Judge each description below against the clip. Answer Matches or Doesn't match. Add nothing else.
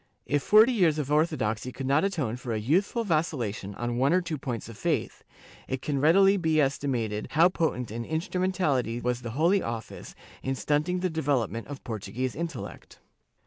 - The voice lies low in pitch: Doesn't match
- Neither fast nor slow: Matches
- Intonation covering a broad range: Matches